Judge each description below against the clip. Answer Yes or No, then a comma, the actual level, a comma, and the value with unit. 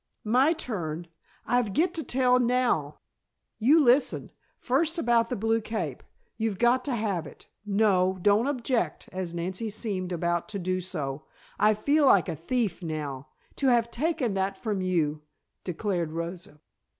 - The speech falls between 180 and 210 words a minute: No, average, 150 wpm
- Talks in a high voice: Yes, high, 210 Hz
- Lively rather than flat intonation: Yes, wide, 5.9 semitones